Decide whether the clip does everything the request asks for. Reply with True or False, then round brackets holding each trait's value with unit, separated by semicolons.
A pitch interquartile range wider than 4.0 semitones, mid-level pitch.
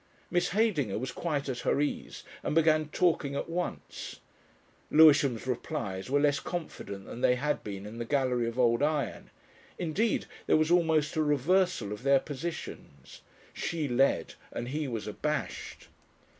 True (4.5 semitones; 145 Hz)